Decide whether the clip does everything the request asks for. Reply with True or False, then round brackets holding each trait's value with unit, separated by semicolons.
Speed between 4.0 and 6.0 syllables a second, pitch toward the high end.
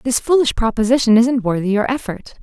True (5.8 syllables/s; 235 Hz)